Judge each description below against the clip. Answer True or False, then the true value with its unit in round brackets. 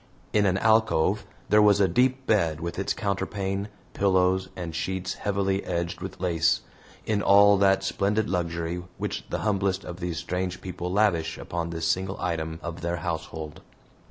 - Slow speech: False (160 wpm)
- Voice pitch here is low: True (95 Hz)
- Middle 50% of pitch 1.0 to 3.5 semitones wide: True (2.8 semitones)